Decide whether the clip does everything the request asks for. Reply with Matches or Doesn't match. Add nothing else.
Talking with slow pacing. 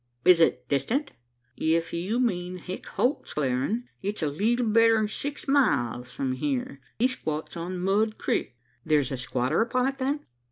Doesn't match